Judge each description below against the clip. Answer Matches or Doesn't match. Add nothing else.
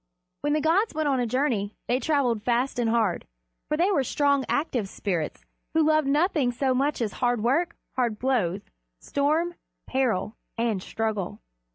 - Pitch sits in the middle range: Doesn't match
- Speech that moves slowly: Doesn't match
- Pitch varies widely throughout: Doesn't match